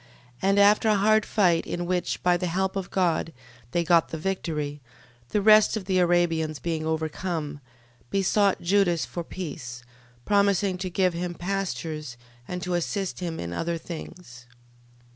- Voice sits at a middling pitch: Yes, medium, 175 Hz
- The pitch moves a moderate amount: Yes, average, 3.0 semitones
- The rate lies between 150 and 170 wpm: Yes, average, 160 wpm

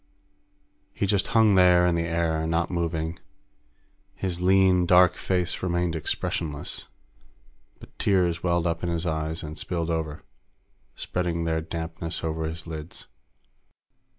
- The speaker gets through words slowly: Yes, slow, 130 wpm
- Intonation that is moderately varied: No, narrow, 1.7 semitones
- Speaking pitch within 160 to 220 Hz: No, very low, 85 Hz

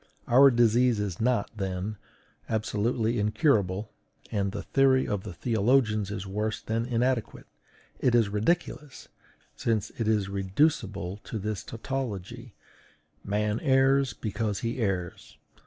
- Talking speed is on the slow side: Yes, slow, 125 wpm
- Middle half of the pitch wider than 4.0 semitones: No, average, 3.3 semitones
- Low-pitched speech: Yes, low, 110 Hz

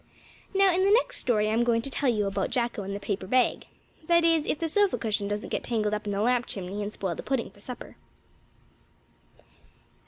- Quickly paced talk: Yes, fast, 215 wpm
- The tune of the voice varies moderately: No, wide, 5.8 semitones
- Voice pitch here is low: No, high, 230 Hz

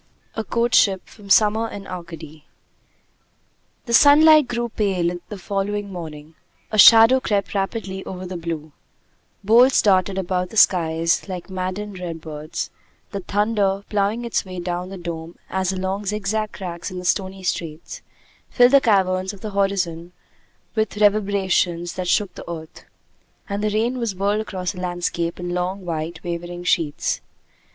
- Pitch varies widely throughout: No, average, 3.1 semitones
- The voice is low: No, high, 190 Hz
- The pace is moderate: Yes, average, 150 wpm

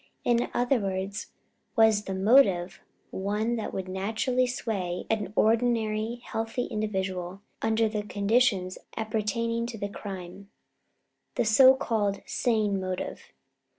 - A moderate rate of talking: No, slow, 120 wpm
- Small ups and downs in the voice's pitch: No, average, 3.0 semitones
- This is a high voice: Yes, high, 215 Hz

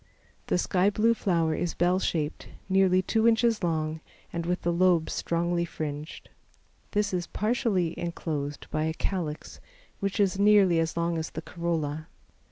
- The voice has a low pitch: No, medium, 175 Hz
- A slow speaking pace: No, average, 155 wpm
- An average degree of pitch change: Yes, average, 3.2 semitones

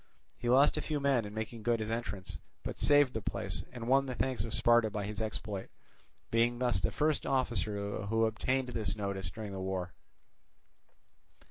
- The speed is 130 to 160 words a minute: No, average, 180 wpm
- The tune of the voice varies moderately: Yes, average, 3.6 semitones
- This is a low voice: Yes, low, 115 Hz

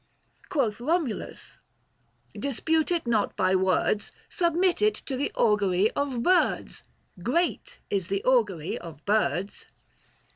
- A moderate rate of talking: No, slow, 130 wpm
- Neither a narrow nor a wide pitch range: No, wide, 8.4 semitones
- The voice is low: No, high, 235 Hz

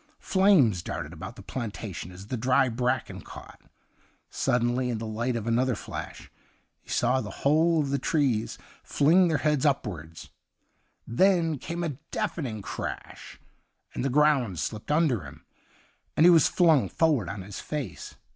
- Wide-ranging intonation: Yes, wide, 5.8 semitones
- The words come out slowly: No, average, 155 wpm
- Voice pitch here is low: Yes, low, 125 Hz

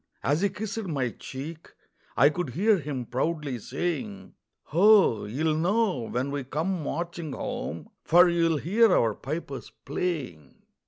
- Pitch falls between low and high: Yes, medium, 155 Hz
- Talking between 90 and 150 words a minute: Yes, average, 140 wpm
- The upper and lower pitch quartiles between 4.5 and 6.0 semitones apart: Yes, average, 5.1 semitones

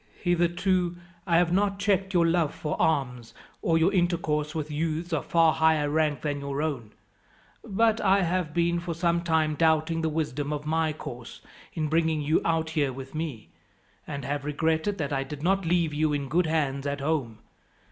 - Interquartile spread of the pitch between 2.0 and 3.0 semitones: Yes, average, 2.7 semitones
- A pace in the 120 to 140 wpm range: No, average, 185 wpm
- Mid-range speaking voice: Yes, medium, 160 Hz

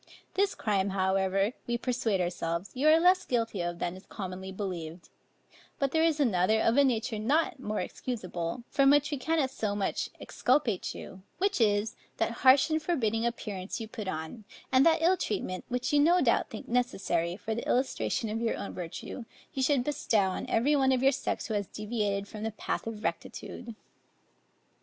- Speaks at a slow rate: No, average, 185 wpm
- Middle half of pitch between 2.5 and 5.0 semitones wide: No, wide, 5.5 semitones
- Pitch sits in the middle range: No, high, 225 Hz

